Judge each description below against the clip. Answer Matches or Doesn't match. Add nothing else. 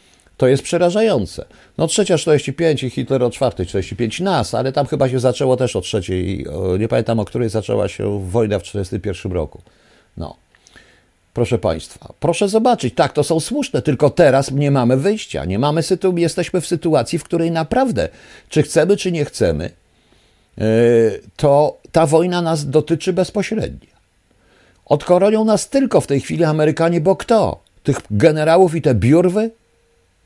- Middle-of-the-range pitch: Matches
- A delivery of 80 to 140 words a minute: Doesn't match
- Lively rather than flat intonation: Matches